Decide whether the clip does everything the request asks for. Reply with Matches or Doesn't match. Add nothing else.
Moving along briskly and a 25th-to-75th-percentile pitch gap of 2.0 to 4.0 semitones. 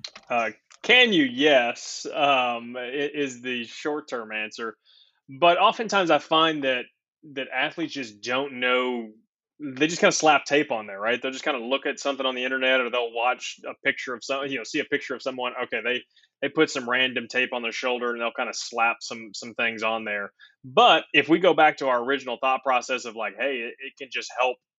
Matches